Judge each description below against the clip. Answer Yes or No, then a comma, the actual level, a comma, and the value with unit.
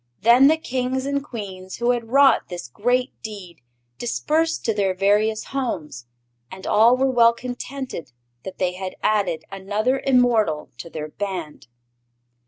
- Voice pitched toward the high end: Yes, high, 220 Hz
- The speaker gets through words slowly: No, average, 145 wpm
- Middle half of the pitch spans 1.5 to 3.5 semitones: No, average, 5.2 semitones